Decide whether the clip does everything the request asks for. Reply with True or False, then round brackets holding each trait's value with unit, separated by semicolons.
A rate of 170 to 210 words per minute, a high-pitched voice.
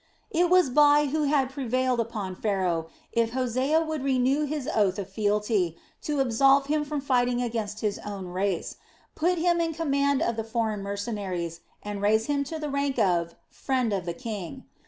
True (180 wpm; 245 Hz)